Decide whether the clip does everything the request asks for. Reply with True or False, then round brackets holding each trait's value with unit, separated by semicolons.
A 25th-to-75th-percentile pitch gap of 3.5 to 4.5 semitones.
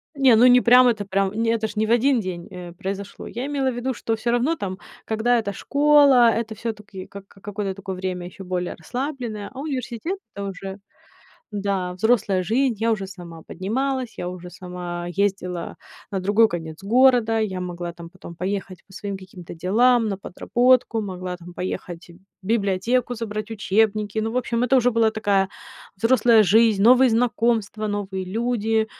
True (4.0 semitones)